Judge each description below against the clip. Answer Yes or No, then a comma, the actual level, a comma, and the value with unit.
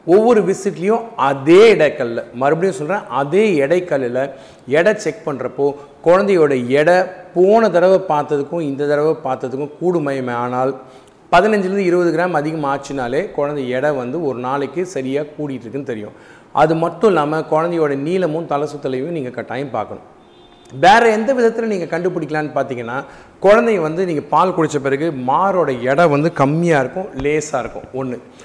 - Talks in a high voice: No, medium, 150 Hz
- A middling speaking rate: No, fast, 135 wpm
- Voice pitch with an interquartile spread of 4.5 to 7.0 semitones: Yes, average, 4.9 semitones